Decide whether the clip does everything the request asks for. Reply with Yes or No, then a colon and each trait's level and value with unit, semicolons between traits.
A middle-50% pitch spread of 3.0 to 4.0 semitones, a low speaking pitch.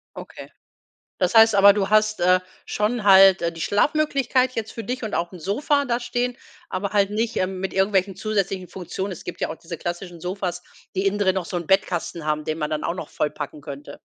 No: average, 3.6 semitones; high, 190 Hz